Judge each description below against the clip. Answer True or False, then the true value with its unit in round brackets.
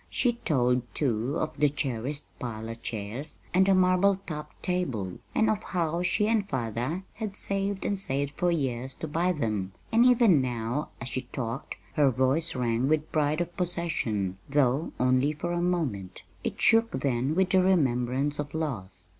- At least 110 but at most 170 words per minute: True (165 wpm)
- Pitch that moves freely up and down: True (6.4 semitones)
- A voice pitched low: False (145 Hz)